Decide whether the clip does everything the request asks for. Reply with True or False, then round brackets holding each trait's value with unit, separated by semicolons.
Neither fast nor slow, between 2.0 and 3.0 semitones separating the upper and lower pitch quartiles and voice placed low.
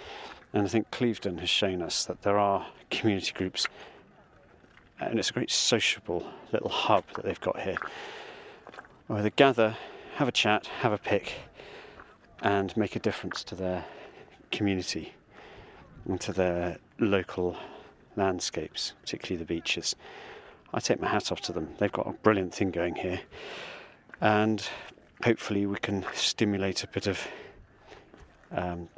True (145 wpm; 2.6 semitones; 100 Hz)